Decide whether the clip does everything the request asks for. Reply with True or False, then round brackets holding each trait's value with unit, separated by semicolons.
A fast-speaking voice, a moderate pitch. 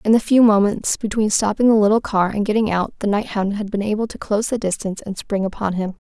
False (245 wpm; 210 Hz)